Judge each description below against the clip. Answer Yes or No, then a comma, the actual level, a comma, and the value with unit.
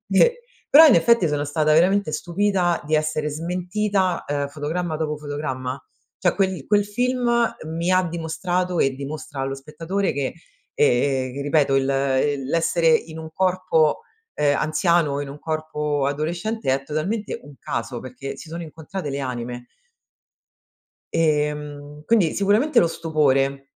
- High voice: No, medium, 155 Hz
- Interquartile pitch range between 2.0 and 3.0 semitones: No, average, 4.0 semitones